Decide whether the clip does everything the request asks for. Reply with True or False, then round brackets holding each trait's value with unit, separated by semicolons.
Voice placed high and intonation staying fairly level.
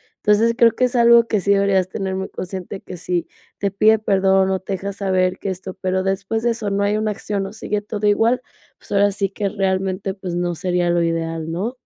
True (195 Hz; 2.0 semitones)